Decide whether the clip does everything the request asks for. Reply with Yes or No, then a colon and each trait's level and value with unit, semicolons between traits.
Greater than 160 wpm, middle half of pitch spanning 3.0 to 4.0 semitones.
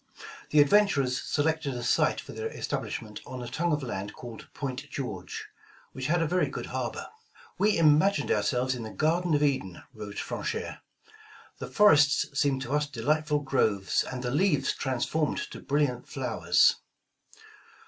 No: average, 155 wpm; average, 3.7 semitones